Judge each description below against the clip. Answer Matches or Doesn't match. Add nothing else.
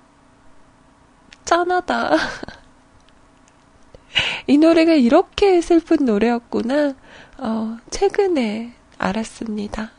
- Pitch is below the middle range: Doesn't match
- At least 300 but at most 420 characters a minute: Doesn't match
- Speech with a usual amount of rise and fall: Doesn't match